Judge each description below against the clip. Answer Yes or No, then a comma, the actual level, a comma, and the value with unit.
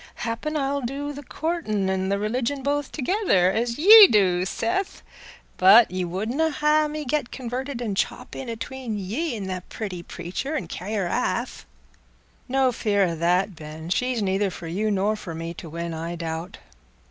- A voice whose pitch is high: Yes, high, 215 Hz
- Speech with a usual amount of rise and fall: No, wide, 6.9 semitones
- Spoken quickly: No, average, 180 wpm